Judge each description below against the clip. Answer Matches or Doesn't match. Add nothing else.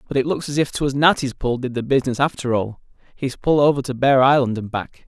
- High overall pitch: Doesn't match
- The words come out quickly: Matches